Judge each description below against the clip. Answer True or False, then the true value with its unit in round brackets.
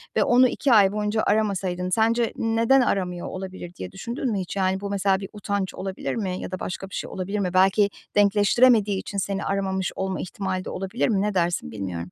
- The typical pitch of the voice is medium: False (195 Hz)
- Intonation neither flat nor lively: False (2.1 semitones)